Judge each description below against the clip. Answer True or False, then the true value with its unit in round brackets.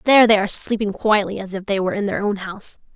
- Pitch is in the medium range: False (205 Hz)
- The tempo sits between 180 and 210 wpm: False (265 wpm)